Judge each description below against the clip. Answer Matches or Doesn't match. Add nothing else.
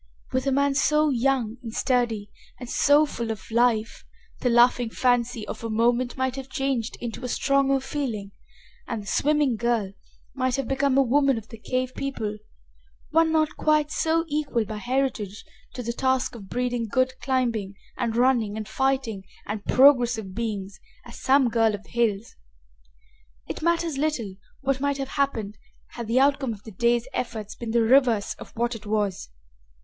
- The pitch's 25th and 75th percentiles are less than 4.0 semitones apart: Matches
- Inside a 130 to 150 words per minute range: Doesn't match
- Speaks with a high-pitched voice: Matches